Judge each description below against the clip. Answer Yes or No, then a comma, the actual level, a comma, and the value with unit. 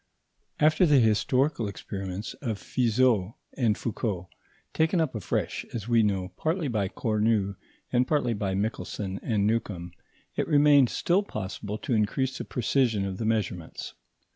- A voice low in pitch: Yes, low, 110 Hz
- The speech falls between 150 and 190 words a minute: No, average, 140 wpm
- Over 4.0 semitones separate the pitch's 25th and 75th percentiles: Yes, average, 4.6 semitones